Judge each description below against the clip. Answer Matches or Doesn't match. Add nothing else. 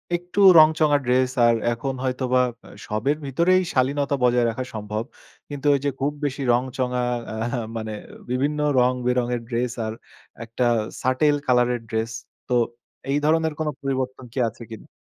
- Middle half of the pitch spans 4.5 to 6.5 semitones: Doesn't match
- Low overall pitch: Matches